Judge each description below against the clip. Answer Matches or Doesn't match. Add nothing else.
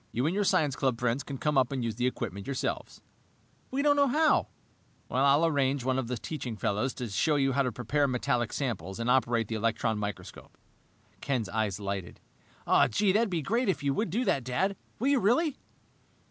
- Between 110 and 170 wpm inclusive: Doesn't match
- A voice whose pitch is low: Matches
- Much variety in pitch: Matches